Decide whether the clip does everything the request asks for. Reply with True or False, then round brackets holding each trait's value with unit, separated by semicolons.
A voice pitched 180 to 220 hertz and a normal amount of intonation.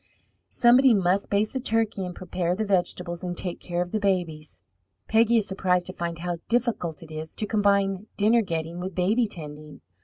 True (185 Hz; 3.7 semitones)